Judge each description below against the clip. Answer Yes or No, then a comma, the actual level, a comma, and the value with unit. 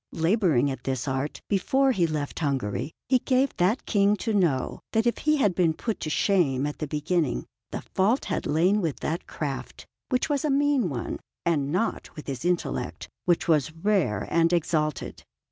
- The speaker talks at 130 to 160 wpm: No, average, 180 wpm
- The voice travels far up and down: Yes, wide, 6.2 semitones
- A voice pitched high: No, medium, 170 Hz